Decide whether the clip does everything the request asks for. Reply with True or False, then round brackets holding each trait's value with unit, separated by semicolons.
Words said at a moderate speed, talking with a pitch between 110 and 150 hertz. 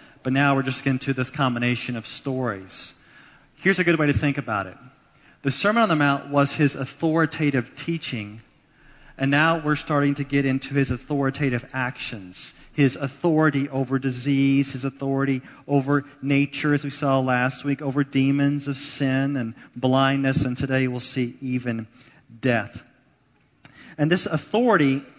True (155 wpm; 135 Hz)